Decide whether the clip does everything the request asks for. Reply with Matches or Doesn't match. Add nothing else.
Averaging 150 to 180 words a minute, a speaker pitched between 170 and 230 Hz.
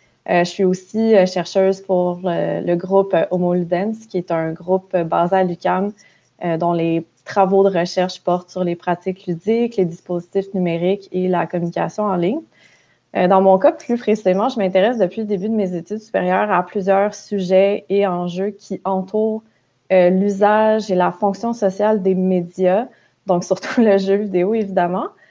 Matches